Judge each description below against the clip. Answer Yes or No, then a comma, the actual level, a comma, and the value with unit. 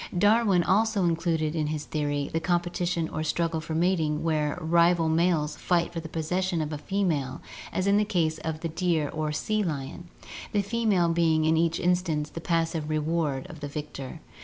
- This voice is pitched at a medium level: Yes, medium, 165 Hz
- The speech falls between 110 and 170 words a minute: No, average, 185 wpm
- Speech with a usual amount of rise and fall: No, narrow, 2.3 semitones